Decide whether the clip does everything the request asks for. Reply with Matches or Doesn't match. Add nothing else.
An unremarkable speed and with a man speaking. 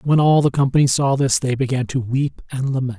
Doesn't match